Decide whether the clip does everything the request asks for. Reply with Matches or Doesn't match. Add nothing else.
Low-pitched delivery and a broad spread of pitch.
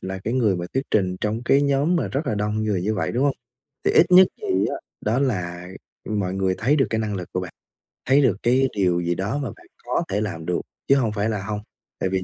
Matches